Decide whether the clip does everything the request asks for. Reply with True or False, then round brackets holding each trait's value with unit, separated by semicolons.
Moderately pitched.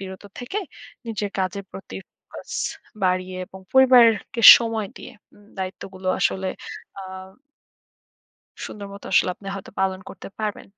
False (195 Hz)